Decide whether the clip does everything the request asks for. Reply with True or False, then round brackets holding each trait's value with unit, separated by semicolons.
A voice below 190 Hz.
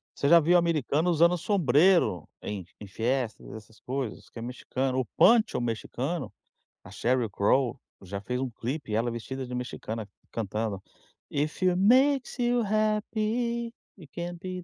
True (135 Hz)